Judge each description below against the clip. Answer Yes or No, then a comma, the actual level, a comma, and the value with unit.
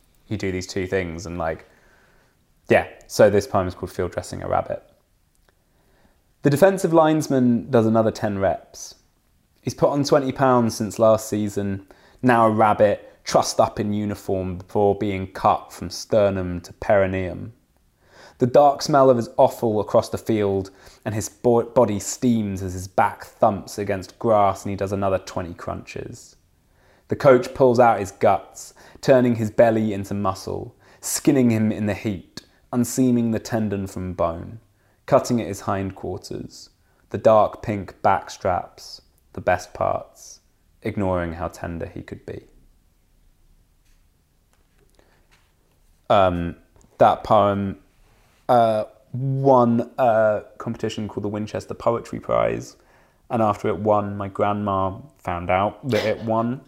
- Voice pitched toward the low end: Yes, low, 105 Hz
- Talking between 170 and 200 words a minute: No, average, 140 wpm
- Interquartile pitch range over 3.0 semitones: Yes, average, 3.5 semitones